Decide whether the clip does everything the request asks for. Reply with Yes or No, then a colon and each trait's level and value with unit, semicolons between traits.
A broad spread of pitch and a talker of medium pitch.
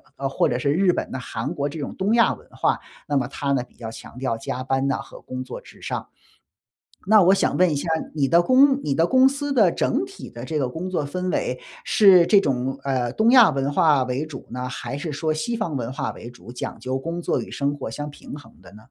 Yes: wide, 6.1 semitones; medium, 145 Hz